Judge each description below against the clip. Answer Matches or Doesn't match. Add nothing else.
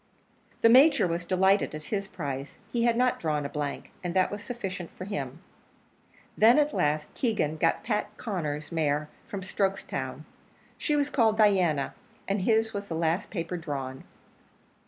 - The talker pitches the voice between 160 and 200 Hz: Matches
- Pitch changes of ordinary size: Doesn't match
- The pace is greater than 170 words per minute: Doesn't match